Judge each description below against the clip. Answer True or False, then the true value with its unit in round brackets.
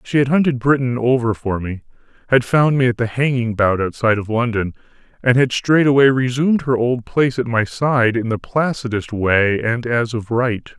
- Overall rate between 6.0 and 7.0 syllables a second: False (5.0 syllables/s)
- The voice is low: True (120 Hz)